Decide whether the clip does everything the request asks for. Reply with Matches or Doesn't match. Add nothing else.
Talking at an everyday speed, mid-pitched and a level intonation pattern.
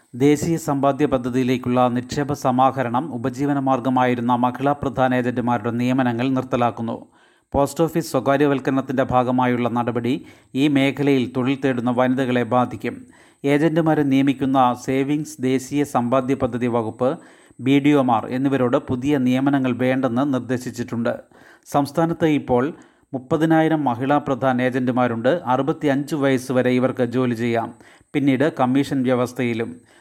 Doesn't match